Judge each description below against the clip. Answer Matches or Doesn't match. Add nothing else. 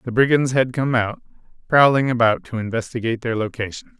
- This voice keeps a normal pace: Matches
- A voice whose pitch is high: Doesn't match